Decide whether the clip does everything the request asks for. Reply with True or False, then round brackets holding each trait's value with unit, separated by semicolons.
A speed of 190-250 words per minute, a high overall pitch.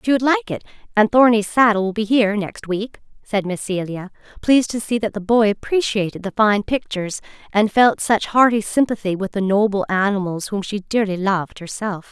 True (195 wpm; 210 Hz)